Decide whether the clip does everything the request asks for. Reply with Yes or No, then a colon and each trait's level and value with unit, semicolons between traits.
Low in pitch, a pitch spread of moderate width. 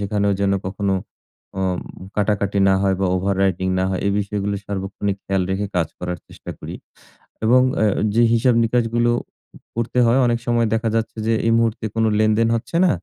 Yes: low, 105 Hz; average, 3.0 semitones